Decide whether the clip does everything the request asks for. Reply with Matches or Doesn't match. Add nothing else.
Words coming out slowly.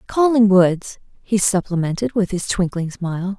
Matches